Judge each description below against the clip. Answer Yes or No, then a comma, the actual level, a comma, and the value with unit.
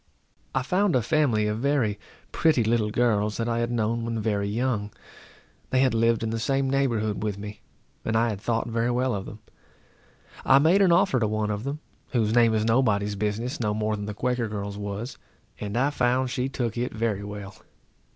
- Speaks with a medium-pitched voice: No, low, 115 Hz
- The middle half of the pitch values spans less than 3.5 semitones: Yes, average, 3.1 semitones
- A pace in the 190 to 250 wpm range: Yes, average, 200 wpm